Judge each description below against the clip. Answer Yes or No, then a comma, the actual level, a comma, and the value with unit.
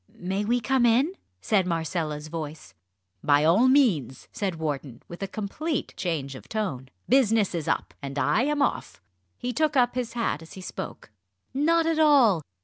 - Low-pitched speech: No, high, 200 Hz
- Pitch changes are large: Yes, wide, 8.4 semitones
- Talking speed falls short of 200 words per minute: Yes, average, 170 wpm